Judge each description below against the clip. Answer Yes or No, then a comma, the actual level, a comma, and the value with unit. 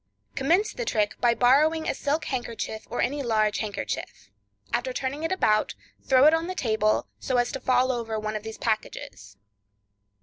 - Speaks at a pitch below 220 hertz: No, high, 245 Hz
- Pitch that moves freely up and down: No, average, 4.8 semitones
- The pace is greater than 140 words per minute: Yes, average, 180 wpm